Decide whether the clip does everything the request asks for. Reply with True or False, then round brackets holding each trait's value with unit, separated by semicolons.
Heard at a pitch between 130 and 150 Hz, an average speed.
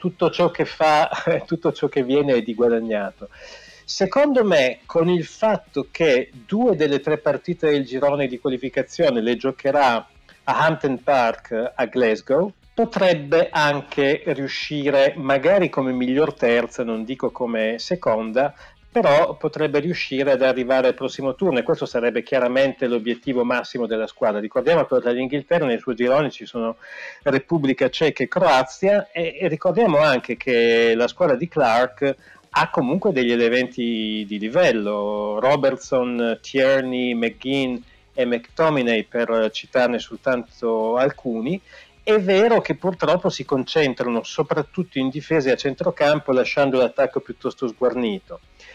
True (135 Hz; 140 wpm)